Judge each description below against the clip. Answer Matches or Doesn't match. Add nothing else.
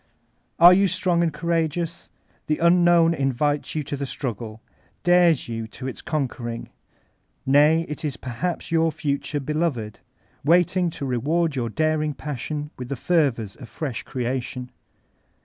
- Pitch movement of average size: Matches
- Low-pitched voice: Doesn't match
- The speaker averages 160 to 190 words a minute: Doesn't match